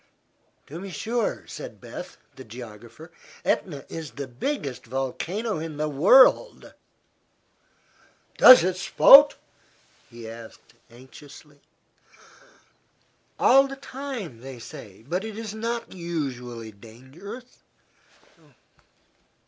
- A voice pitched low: No, medium, 155 Hz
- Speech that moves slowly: Yes, slow, 100 wpm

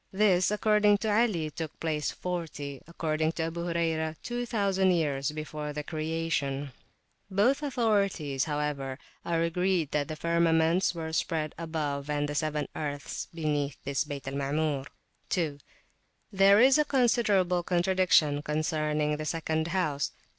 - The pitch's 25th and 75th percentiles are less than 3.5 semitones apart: No, average, 3.8 semitones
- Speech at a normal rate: No, slow, 130 wpm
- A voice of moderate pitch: Yes, medium, 160 Hz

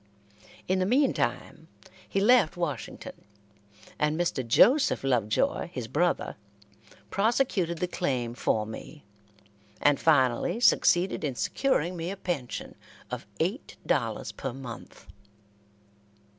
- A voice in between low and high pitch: Yes, medium, 170 Hz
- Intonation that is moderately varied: No, wide, 6.7 semitones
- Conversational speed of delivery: No, slow, 110 wpm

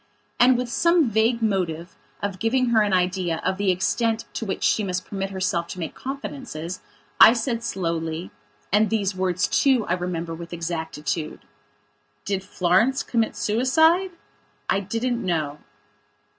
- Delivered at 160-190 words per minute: No, average, 145 wpm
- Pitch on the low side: No, high, 195 Hz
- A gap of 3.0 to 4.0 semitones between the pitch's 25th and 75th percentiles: No, average, 5.0 semitones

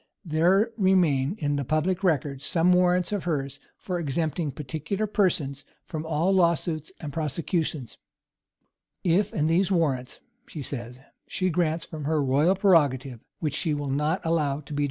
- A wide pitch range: No, average, 3.8 semitones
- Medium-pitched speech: Yes, medium, 160 Hz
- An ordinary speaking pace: Yes, average, 160 wpm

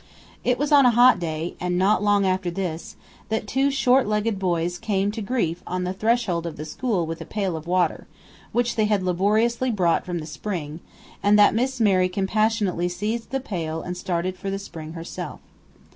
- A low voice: No, high, 195 Hz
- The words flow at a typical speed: Yes, average, 195 wpm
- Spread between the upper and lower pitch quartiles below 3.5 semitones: No, average, 4.1 semitones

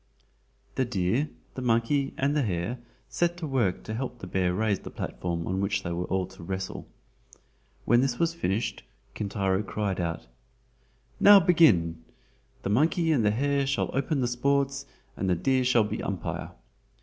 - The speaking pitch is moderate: No, low, 115 Hz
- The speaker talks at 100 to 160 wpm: No, average, 170 wpm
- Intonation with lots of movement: Yes, wide, 6.5 semitones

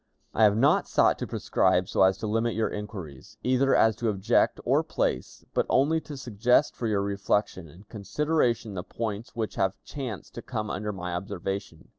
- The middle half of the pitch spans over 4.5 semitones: No, average, 3.4 semitones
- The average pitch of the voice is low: Yes, low, 105 Hz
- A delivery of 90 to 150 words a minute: No, average, 185 wpm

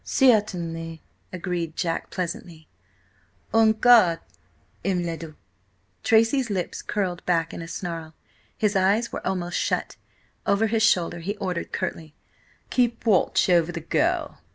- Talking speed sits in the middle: No, slow, 130 wpm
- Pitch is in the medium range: Yes, medium, 180 Hz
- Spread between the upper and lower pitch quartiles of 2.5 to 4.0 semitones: No, average, 4.6 semitones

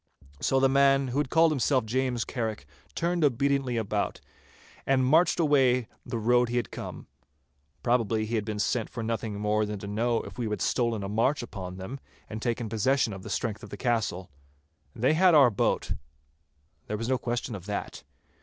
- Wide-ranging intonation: No, average, 3.9 semitones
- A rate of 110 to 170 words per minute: No, average, 185 wpm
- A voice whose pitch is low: Yes, low, 120 Hz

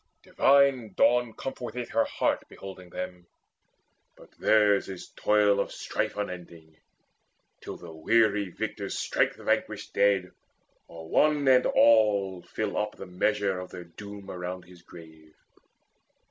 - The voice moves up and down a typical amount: Yes, average, 3.4 semitones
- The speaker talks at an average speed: No, slow, 130 wpm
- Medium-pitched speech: No, low, 100 Hz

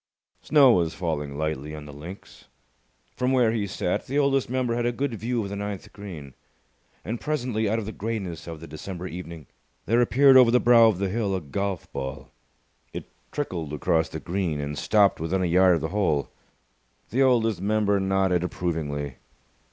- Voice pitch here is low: Yes, very low, 95 Hz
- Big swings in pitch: Yes, wide, 6.0 semitones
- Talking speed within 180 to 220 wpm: Yes, average, 185 wpm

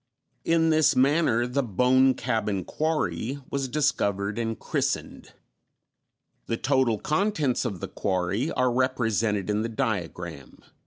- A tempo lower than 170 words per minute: Yes, slow, 135 wpm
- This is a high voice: No, low, 120 Hz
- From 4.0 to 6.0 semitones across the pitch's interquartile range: Yes, average, 5.0 semitones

